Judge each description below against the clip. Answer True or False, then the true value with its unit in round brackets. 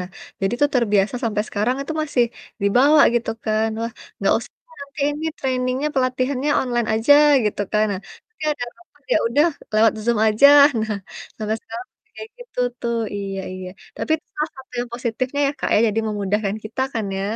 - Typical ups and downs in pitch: True (4.5 semitones)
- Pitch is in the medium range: False (235 Hz)